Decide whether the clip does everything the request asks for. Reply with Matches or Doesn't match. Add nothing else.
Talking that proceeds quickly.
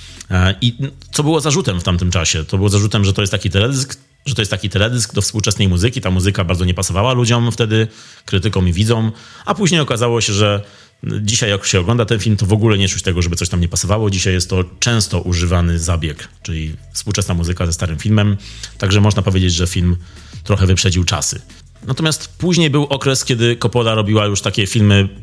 Matches